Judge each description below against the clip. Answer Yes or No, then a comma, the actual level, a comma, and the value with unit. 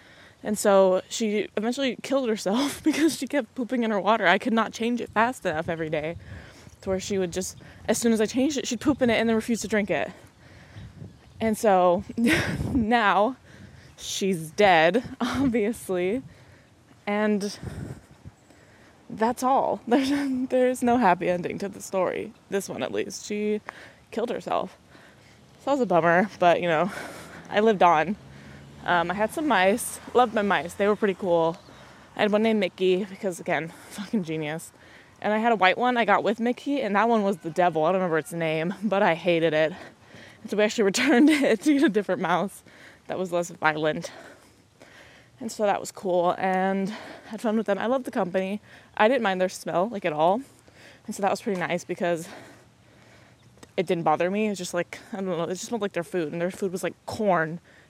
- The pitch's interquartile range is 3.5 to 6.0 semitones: Yes, average, 4.3 semitones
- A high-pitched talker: Yes, high, 200 Hz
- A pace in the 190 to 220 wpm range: Yes, average, 200 wpm